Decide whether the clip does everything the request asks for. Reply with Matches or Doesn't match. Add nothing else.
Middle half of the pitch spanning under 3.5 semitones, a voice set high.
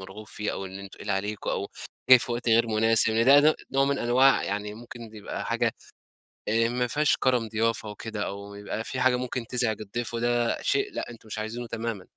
Doesn't match